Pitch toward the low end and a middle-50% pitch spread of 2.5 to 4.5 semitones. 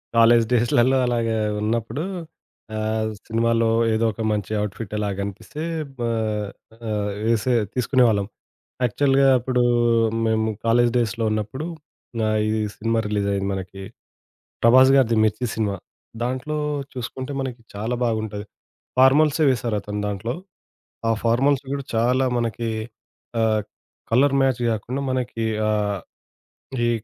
Yes: low, 115 Hz; average, 2.8 semitones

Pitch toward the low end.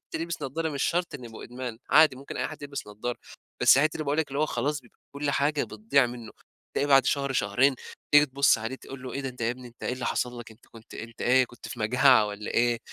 Yes: low, 130 Hz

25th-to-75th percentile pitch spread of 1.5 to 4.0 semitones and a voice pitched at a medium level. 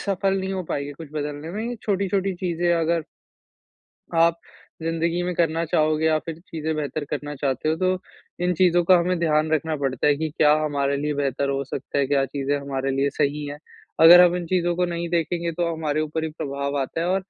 Yes: average, 3.2 semitones; medium, 160 Hz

